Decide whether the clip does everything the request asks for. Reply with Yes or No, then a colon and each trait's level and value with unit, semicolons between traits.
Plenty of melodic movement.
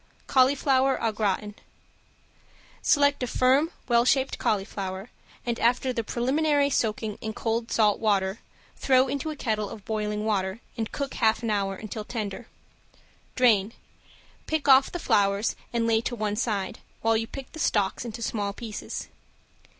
No: average, 3.7 semitones